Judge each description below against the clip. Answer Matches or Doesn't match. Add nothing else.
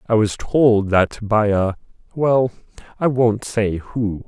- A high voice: Doesn't match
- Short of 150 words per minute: Matches